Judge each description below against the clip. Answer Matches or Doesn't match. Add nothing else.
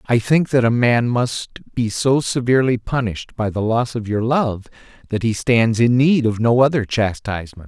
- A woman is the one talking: Doesn't match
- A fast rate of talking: Doesn't match